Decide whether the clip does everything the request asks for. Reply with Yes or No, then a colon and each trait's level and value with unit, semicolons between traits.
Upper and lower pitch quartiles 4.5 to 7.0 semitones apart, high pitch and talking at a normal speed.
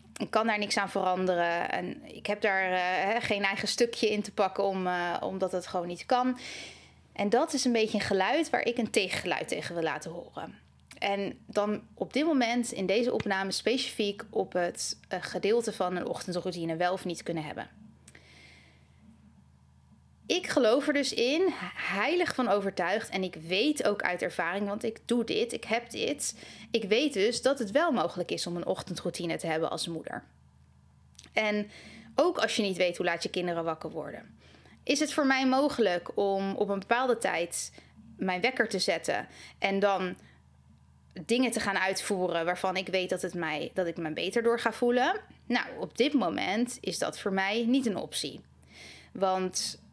Yes: average, 5.2 semitones; high, 195 Hz; average, 185 wpm